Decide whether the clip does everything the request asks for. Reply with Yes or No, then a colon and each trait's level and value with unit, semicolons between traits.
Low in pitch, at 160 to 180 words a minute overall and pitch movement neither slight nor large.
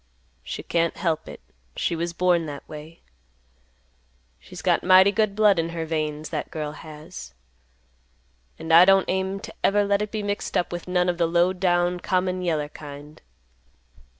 No: medium, 175 Hz; average, 170 wpm; average, 3.0 semitones